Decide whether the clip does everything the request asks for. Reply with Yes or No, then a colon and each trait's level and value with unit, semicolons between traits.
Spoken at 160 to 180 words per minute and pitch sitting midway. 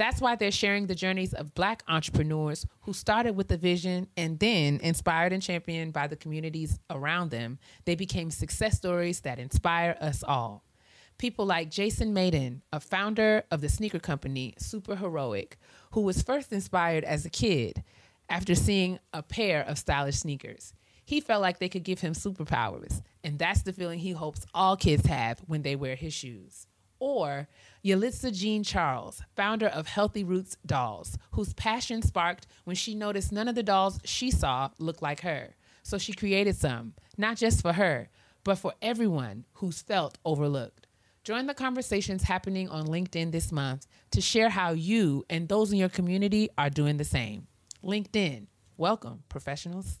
Yes: average, 170 wpm; medium, 170 Hz